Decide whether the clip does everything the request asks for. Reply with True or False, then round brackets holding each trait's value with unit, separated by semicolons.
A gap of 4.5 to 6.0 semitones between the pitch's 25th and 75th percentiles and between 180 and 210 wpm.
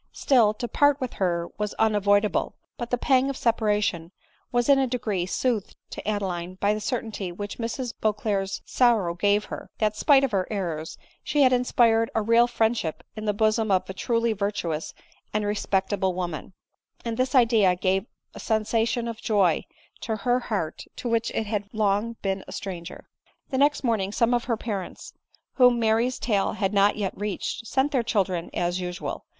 False (3.4 semitones; 185 wpm)